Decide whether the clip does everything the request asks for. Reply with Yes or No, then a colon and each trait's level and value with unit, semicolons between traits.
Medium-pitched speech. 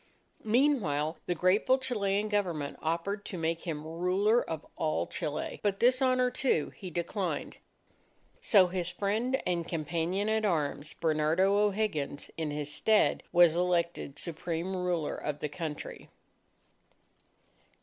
Yes: medium, 180 Hz